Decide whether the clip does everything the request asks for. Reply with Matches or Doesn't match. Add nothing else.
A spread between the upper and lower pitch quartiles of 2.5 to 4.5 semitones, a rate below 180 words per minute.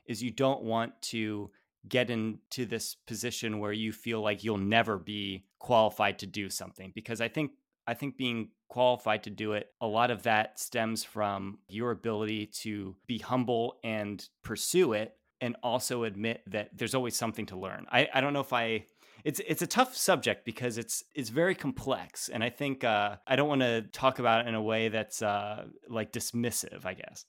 Doesn't match